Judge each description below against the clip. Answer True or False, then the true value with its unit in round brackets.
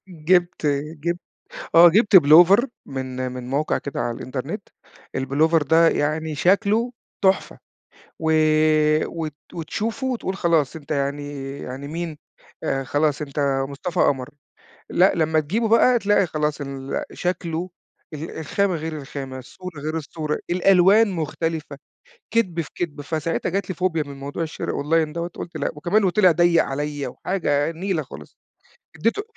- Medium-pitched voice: True (160 Hz)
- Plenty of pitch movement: False (3.8 semitones)